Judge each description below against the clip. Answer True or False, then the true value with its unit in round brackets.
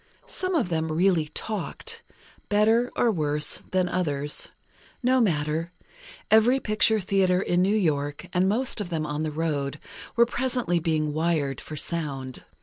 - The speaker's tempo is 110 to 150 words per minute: True (145 wpm)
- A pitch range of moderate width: False (5.9 semitones)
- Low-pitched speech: False (175 Hz)